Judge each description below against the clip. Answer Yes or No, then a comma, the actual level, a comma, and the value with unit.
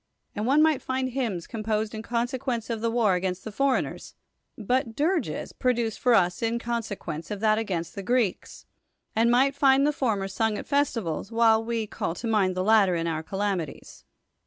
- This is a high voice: Yes, high, 225 Hz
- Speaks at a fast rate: No, average, 190 wpm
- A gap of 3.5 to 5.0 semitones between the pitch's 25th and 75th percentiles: Yes, average, 4.0 semitones